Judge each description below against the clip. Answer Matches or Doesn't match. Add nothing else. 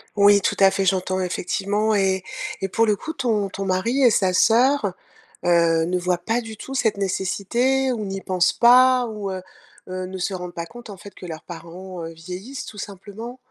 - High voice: Matches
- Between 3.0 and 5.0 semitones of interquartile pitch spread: Matches